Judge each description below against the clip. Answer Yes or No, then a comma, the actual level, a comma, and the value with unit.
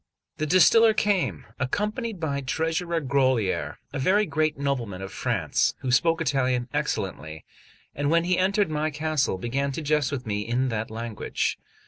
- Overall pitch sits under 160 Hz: Yes, medium, 140 Hz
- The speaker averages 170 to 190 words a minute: No, average, 155 wpm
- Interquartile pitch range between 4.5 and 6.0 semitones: Yes, average, 4.9 semitones